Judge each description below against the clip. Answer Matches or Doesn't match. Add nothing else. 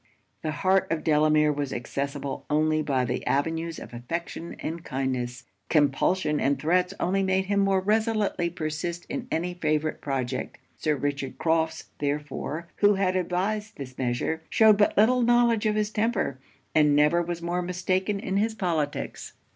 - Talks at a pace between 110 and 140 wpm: Doesn't match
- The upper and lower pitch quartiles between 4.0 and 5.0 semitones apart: Matches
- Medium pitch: Matches